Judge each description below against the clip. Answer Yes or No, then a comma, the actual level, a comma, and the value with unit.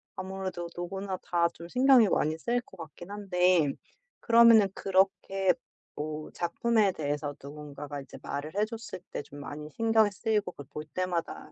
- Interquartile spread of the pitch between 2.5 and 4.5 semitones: No, average, 5.2 semitones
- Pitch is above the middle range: No, medium, 180 Hz